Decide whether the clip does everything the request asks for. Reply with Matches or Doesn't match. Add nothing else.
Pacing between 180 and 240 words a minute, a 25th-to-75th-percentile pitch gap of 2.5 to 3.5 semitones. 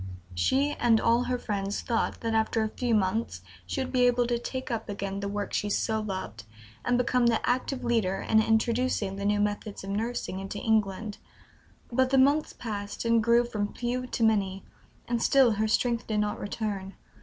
Matches